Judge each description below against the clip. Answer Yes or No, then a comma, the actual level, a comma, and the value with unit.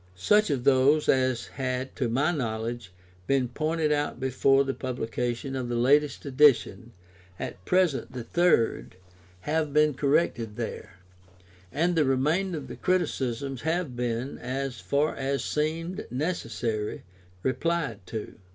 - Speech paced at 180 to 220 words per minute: No, slow, 135 wpm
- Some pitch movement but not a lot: Yes, average, 3.8 semitones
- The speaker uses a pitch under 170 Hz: Yes, low, 135 Hz